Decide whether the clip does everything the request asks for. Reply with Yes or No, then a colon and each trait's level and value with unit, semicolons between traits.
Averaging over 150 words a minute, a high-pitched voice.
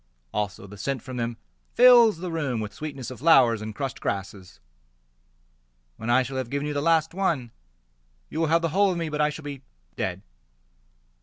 No: average, 190 wpm; medium, 140 Hz